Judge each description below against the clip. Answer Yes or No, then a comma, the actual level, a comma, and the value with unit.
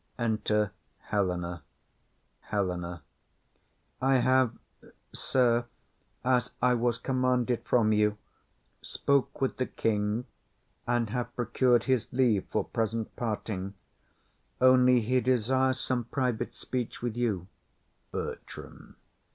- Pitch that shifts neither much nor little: Yes, average, 3.1 semitones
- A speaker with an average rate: No, slow, 100 wpm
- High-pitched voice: No, low, 120 Hz